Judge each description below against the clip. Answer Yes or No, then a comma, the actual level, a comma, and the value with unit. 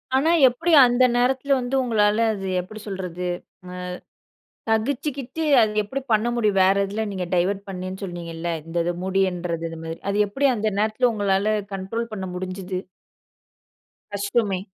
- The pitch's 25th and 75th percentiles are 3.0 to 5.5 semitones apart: Yes, average, 4.0 semitones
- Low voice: No, high, 205 Hz